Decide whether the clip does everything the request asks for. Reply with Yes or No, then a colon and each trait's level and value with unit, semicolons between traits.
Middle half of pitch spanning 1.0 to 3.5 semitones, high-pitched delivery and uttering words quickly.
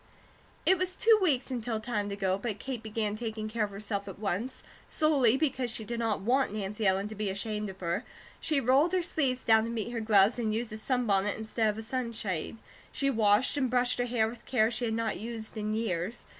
Yes: average, 2.9 semitones; high, 225 Hz; fast, 225 wpm